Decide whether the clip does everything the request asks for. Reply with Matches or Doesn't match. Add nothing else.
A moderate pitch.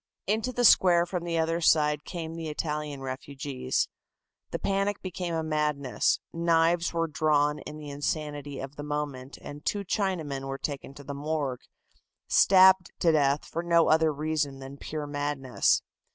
Matches